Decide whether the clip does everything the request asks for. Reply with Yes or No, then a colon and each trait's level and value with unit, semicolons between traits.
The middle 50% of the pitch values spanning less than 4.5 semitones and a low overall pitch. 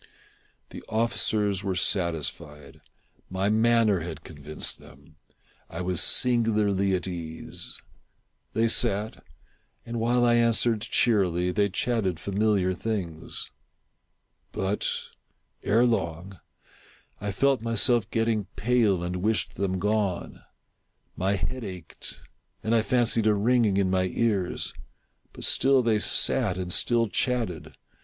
Yes: average, 4.1 semitones; low, 100 Hz